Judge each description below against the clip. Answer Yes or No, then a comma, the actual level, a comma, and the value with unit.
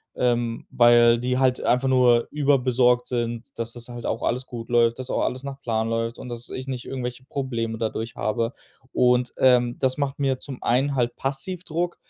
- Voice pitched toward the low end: Yes, low, 125 Hz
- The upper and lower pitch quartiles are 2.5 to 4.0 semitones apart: No, narrow, 1.9 semitones